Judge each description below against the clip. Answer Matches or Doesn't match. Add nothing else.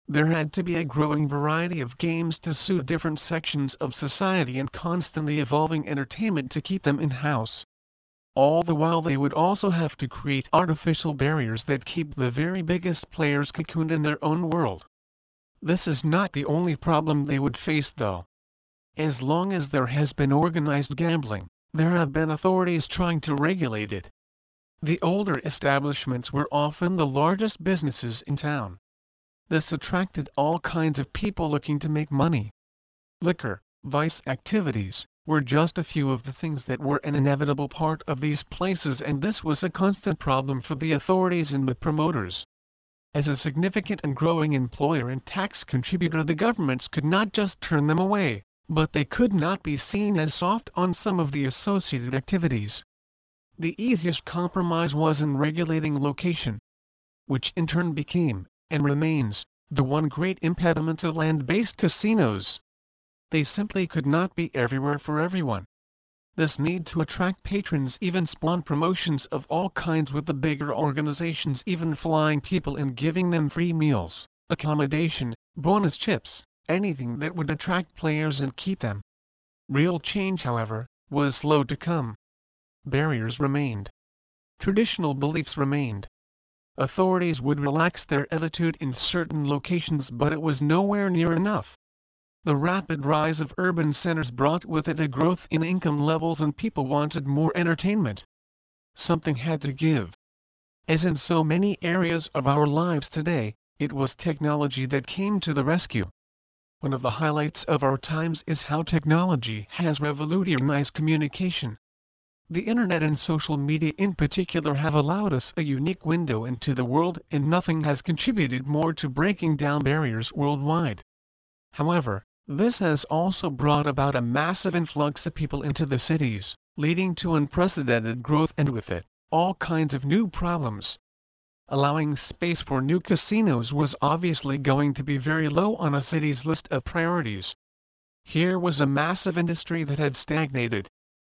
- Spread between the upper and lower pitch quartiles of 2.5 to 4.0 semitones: Matches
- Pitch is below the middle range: Doesn't match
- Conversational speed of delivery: Matches